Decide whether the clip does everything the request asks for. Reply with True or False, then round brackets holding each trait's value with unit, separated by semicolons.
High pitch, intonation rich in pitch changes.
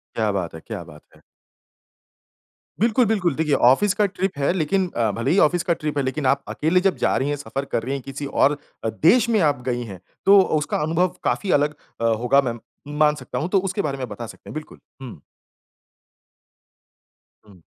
False (145 Hz; 6.0 semitones)